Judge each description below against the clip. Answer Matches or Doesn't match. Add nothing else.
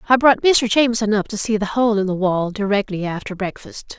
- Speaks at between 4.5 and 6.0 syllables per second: Matches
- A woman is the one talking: Matches